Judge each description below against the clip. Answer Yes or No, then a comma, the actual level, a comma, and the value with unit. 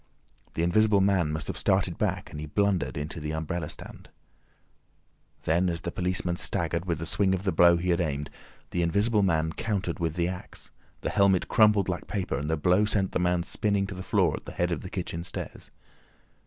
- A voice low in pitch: Yes, very low, 90 Hz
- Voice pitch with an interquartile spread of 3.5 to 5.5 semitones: No, average, 2.8 semitones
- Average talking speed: No, fast, 210 wpm